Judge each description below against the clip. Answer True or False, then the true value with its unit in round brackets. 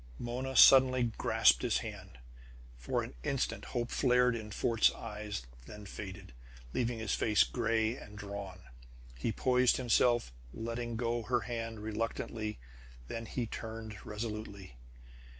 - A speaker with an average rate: False (130 wpm)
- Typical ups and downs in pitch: False (2.3 semitones)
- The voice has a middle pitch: False (115 Hz)